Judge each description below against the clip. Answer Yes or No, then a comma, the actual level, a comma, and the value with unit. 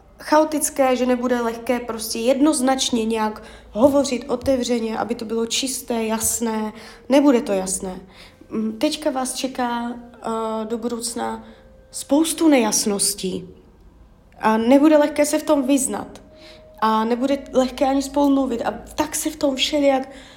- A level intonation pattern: No, average, 3.8 semitones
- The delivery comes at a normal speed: Yes, average, 125 wpm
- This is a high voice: Yes, very high, 250 Hz